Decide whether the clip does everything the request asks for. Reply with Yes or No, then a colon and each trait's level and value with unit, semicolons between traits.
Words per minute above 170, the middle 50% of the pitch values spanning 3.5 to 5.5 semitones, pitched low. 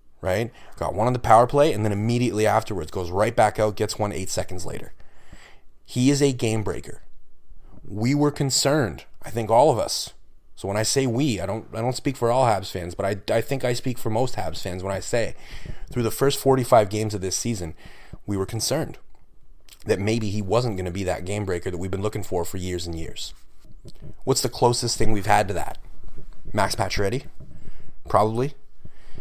Yes: fast, 205 wpm; average, 4.5 semitones; low, 110 Hz